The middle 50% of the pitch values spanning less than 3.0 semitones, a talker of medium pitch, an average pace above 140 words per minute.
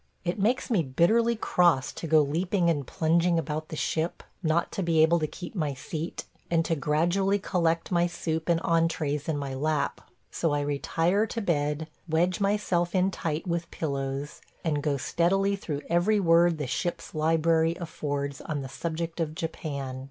Yes: narrow, 2.5 semitones; medium, 165 Hz; average, 175 wpm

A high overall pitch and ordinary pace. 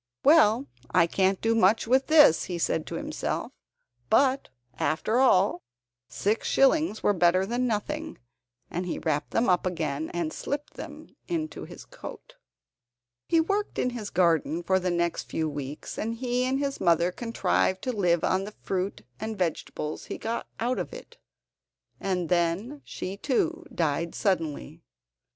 Yes: high, 195 Hz; average, 155 wpm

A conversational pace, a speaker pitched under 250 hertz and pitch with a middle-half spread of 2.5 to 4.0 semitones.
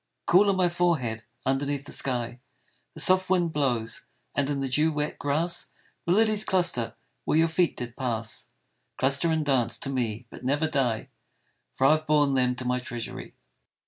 No: average, 175 wpm; medium, 140 Hz; average, 4.7 semitones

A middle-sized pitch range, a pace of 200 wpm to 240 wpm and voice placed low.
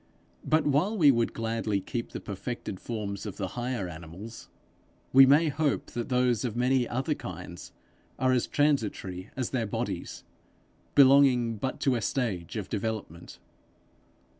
No: average, 4.7 semitones; average, 145 wpm; low, 120 Hz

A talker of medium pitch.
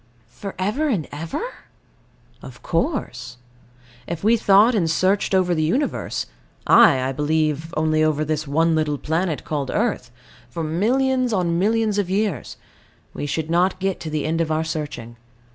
Yes: medium, 165 Hz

